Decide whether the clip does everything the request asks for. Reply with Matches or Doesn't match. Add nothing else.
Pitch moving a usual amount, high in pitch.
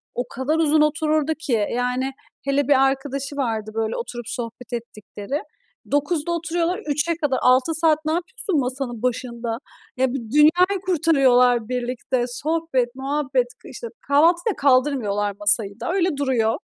Matches